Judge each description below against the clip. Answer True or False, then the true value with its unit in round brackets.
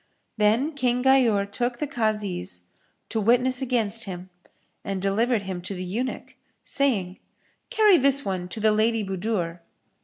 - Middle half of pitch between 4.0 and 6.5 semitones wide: True (4.6 semitones)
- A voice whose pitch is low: False (220 Hz)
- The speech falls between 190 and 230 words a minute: False (145 wpm)